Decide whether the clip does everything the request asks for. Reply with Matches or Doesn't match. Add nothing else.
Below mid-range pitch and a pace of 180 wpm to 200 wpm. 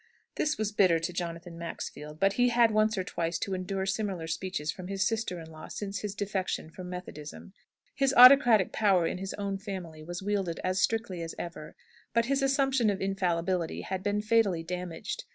Doesn't match